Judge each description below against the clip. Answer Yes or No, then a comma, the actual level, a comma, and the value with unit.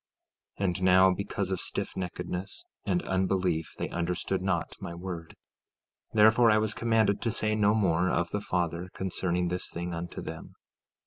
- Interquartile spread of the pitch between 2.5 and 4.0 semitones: Yes, average, 2.8 semitones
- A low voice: Yes, very low, 95 Hz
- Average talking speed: Yes, average, 155 wpm